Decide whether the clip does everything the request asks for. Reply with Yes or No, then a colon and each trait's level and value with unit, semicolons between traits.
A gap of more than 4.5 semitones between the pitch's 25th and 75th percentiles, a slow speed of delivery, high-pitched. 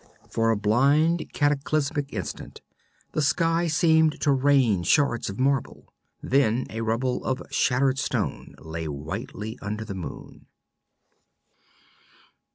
No: average, 5.0 semitones; slow, 115 wpm; low, 130 Hz